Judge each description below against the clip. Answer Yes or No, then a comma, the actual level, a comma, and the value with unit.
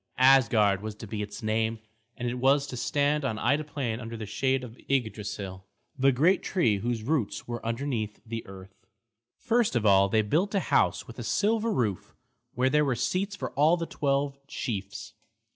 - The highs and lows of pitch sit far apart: No, average, 4.9 semitones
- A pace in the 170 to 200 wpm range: Yes, average, 185 wpm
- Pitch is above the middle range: No, low, 125 Hz